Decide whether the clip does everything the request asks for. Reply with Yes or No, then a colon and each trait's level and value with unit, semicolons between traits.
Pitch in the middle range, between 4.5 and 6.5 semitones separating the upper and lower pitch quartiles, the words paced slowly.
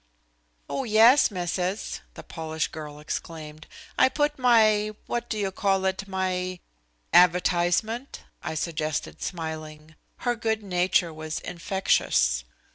Yes: medium, 180 Hz; average, 5.2 semitones; slow, 120 wpm